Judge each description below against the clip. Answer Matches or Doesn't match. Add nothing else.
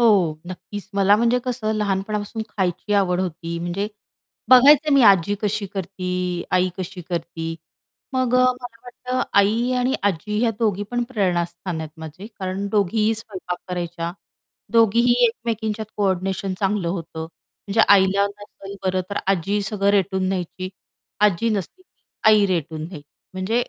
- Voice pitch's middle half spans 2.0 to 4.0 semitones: Matches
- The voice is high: Matches